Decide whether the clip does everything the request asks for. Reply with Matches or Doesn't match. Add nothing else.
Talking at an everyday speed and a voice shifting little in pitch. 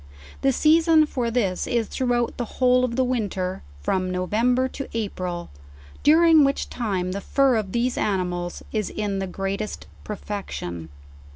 Doesn't match